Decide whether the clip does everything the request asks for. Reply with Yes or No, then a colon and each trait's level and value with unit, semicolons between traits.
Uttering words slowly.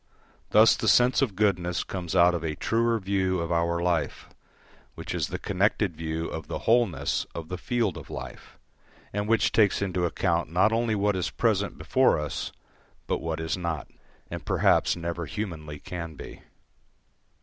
No: average, 170 wpm